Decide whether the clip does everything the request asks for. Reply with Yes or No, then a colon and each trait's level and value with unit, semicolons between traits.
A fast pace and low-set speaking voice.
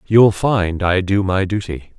No: average, 180 wpm; very low, 95 Hz